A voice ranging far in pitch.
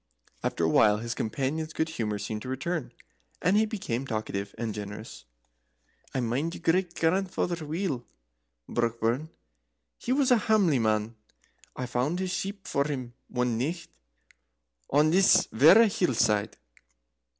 Yes: wide, 7.6 semitones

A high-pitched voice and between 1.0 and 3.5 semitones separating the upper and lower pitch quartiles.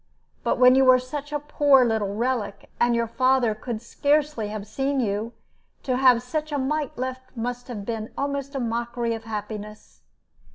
Yes: high, 245 Hz; average, 3.1 semitones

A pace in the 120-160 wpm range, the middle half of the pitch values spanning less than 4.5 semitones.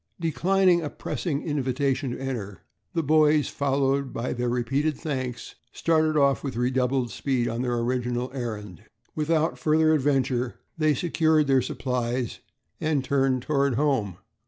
Yes: slow, 135 wpm; average, 3.6 semitones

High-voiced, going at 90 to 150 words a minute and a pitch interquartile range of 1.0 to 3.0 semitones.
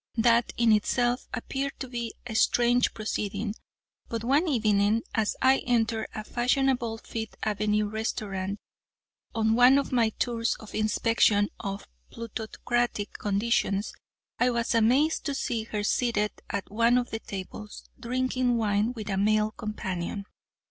Yes: high, 225 Hz; average, 140 wpm; narrow, 2.4 semitones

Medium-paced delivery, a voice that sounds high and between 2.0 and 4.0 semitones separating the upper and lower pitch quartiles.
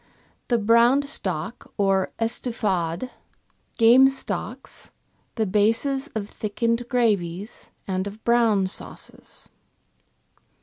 No: slow, 95 wpm; high, 225 Hz; average, 3.5 semitones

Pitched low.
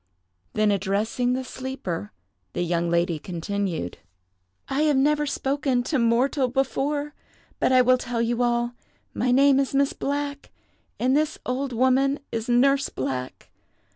No: very high, 255 Hz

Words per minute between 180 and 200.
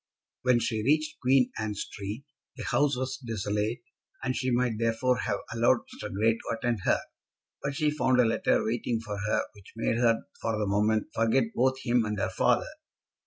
Yes: average, 185 wpm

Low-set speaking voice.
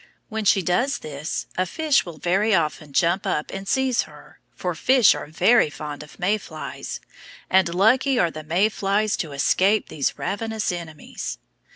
No: medium, 185 Hz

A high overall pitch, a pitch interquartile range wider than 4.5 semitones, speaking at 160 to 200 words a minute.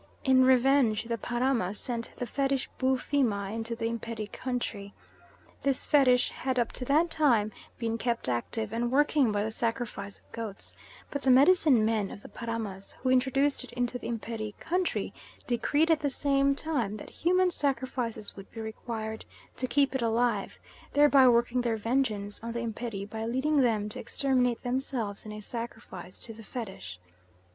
No: high, 235 Hz; average, 3.4 semitones; average, 165 wpm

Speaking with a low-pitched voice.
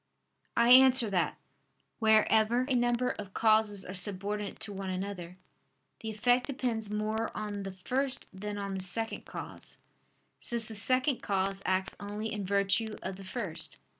No: high, 210 Hz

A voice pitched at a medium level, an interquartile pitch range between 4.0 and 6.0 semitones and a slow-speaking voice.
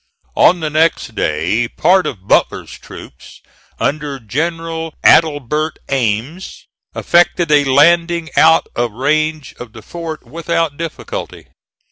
Yes: medium, 155 Hz; average, 4.3 semitones; slow, 115 wpm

